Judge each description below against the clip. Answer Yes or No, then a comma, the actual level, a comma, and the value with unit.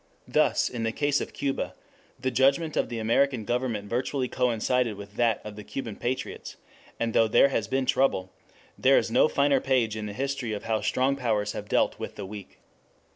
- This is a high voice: No, low, 120 Hz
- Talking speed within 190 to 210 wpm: Yes, average, 195 wpm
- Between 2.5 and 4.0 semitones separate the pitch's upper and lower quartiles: Yes, average, 3.7 semitones